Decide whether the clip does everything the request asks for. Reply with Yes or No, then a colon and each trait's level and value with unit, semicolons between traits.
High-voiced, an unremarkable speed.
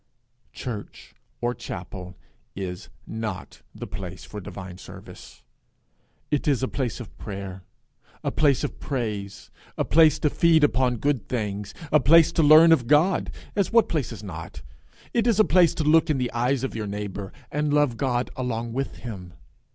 No: low, 125 Hz; average, 170 wpm